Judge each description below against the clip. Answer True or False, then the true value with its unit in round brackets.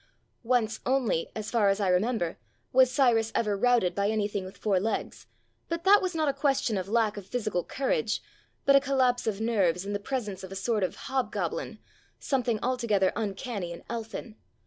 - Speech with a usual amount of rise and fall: True (4.2 semitones)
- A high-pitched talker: True (225 Hz)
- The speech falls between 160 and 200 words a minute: True (185 wpm)